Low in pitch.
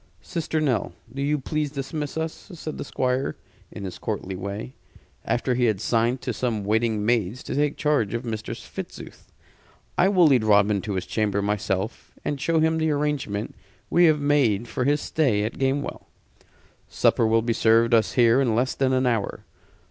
Yes: low, 125 Hz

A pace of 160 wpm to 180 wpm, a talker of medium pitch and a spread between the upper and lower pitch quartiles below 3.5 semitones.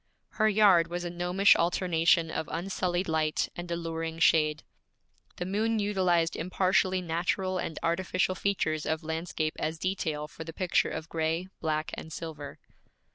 No: average, 145 wpm; medium, 170 Hz; narrow, 2.4 semitones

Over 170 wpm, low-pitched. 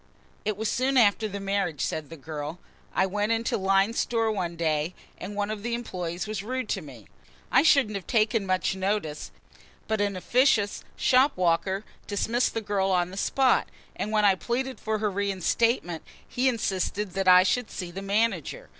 No: average, 180 wpm; high, 200 Hz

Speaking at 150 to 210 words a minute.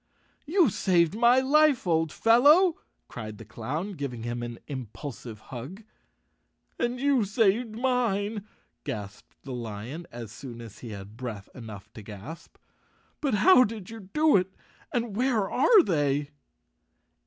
No: average, 140 wpm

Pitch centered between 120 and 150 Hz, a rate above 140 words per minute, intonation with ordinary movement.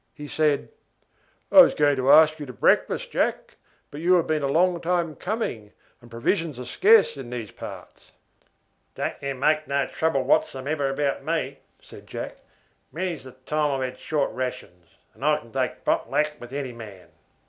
Yes: medium, 140 Hz; average, 175 wpm; average, 3.6 semitones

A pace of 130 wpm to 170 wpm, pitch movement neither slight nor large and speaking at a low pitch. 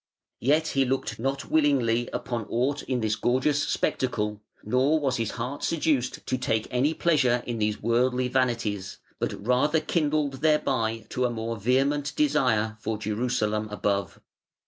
Yes: average, 145 wpm; average, 3.9 semitones; low, 125 Hz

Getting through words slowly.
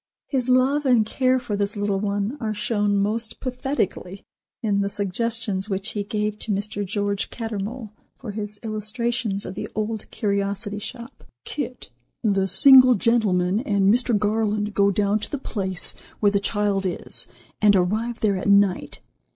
No: average, 160 wpm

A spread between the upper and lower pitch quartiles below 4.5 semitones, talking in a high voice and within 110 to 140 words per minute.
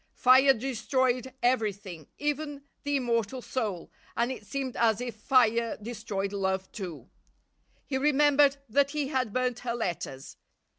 Yes: average, 4.1 semitones; high, 245 Hz; slow, 135 wpm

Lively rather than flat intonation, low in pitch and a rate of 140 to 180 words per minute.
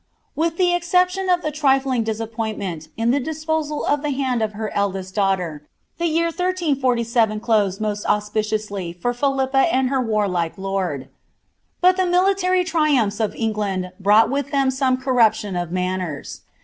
No: wide, 6.7 semitones; high, 235 Hz; average, 150 wpm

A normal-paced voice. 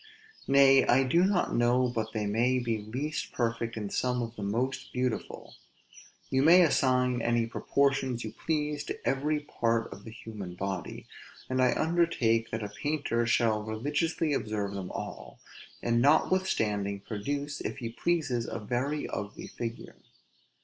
Yes: average, 150 wpm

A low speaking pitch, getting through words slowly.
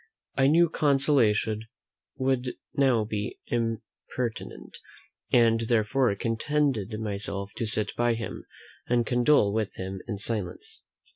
Yes: low, 115 Hz; slow, 115 wpm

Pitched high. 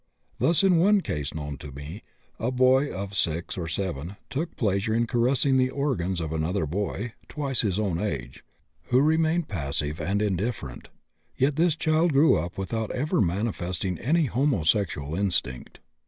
No: low, 105 Hz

